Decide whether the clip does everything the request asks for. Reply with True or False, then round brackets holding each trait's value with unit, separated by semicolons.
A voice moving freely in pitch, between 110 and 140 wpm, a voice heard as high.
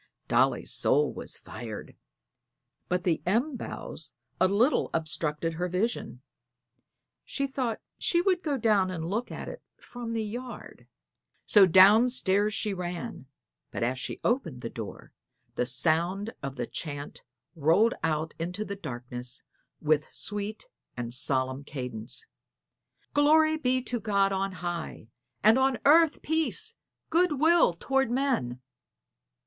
True (8.2 semitones; 135 wpm; 195 Hz)